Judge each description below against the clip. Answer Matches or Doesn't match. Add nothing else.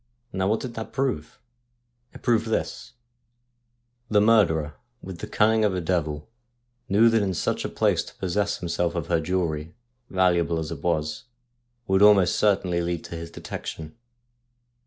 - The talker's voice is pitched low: Matches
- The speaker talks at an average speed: Matches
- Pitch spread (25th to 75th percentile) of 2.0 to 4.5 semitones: Matches